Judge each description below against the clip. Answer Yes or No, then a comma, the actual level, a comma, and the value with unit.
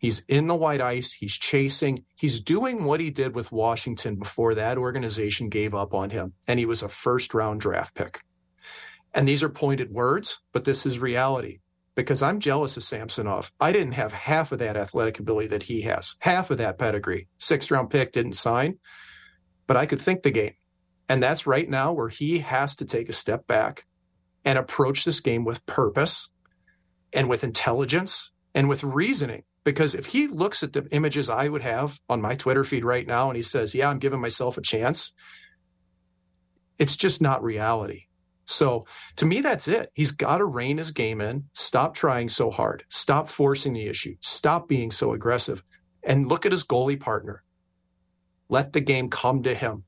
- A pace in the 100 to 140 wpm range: No, average, 190 wpm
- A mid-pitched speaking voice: No, low, 125 Hz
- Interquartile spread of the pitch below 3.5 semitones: No, average, 5.1 semitones